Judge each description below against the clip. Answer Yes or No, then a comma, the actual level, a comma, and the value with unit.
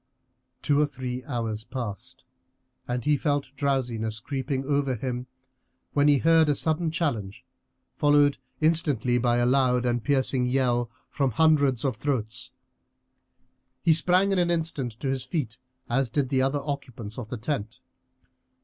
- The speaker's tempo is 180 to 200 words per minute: No, average, 150 wpm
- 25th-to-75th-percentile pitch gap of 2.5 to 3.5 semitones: Yes, average, 3.2 semitones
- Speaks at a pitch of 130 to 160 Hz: Yes, low, 135 Hz